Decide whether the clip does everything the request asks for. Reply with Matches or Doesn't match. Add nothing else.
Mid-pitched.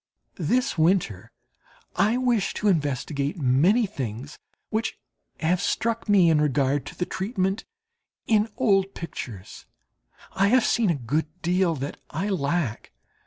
Matches